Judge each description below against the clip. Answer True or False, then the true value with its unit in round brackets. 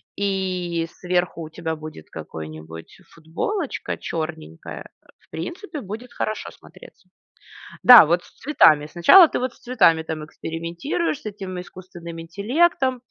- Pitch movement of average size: False (7.0 semitones)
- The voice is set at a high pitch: False (175 Hz)